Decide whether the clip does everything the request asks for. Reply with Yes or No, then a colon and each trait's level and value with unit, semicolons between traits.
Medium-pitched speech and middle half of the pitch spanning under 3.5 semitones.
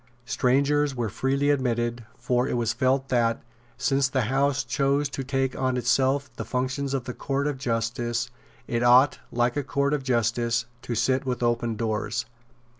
No: low, 130 Hz; narrow, 2.5 semitones